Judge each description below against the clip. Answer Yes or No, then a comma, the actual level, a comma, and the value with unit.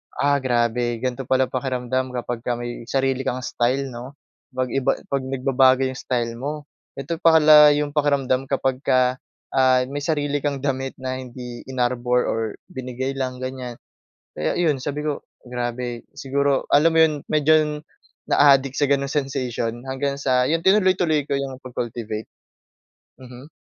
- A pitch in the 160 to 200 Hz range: No, low, 130 Hz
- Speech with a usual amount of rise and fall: No, narrow, 2.2 semitones